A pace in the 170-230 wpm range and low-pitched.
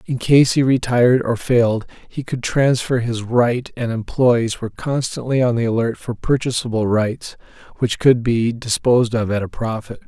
Yes: average, 175 wpm; low, 120 Hz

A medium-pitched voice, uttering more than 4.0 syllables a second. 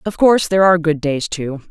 Yes: medium, 170 Hz; 6.5 syllables/s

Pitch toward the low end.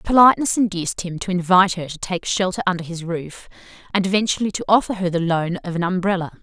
No: medium, 185 Hz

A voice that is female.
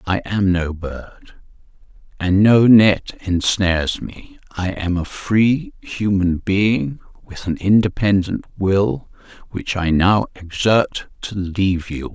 No: male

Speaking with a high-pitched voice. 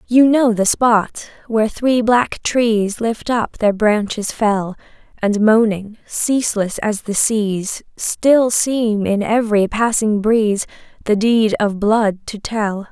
Yes: high, 220 Hz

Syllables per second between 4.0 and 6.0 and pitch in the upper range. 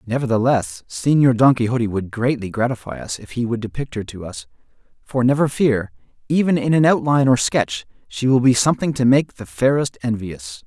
No: 5.4 syllables/s; low, 120 Hz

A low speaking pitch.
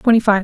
No: high, 215 Hz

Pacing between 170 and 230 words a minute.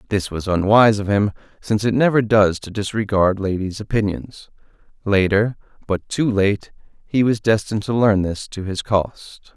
No: average, 155 wpm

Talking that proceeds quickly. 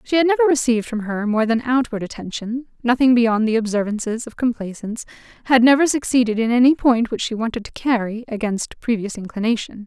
No: average, 185 wpm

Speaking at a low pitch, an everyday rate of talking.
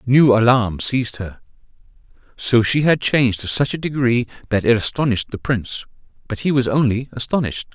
Yes: low, 120 Hz; average, 170 wpm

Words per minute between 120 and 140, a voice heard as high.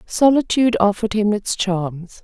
Yes: slow, 135 wpm; high, 210 Hz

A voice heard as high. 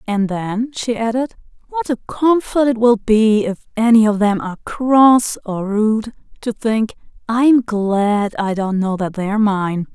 Yes: high, 220 Hz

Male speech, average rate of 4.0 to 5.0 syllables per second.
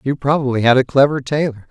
No: male; 6.2 syllables/s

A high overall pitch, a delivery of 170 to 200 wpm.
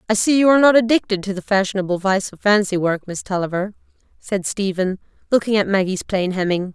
Yes: high, 200 Hz; average, 195 wpm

